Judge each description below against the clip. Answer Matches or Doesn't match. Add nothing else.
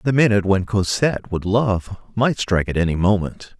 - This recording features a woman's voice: Doesn't match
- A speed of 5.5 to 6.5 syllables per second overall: Matches